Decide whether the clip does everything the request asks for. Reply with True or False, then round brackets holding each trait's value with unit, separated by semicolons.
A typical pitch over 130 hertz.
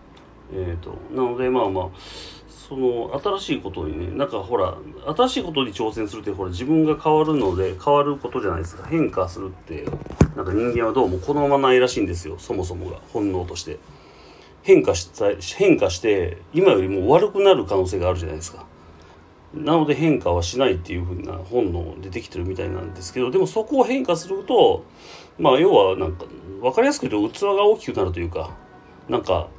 False (120 Hz)